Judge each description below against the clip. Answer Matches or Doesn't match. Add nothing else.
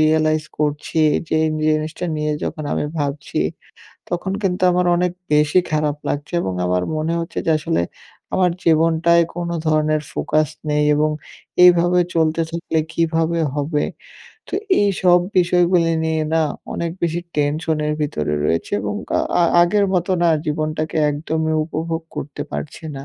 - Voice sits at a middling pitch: Matches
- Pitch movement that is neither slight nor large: Doesn't match